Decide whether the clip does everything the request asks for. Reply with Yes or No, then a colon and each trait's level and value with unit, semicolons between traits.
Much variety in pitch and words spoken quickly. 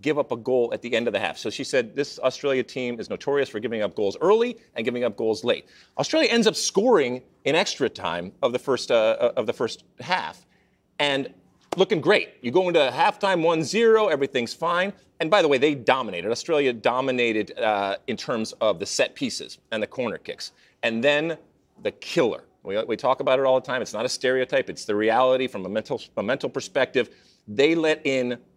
Yes: wide, 6.7 semitones; fast, 210 wpm